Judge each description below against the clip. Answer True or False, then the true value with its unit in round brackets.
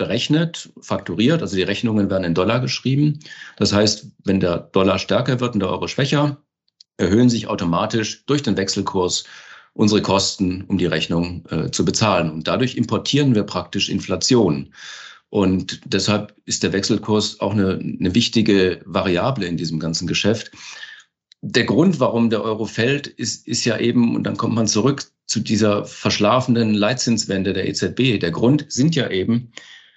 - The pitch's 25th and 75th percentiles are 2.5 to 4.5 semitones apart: True (3.9 semitones)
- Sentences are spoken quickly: False (160 wpm)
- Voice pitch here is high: False (105 Hz)